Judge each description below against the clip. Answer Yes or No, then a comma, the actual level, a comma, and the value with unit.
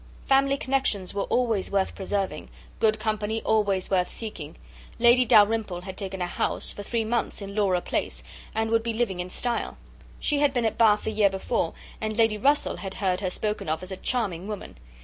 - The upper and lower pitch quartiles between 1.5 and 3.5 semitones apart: Yes, average, 3.0 semitones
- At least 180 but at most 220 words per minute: Yes, average, 195 wpm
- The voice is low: No, high, 210 Hz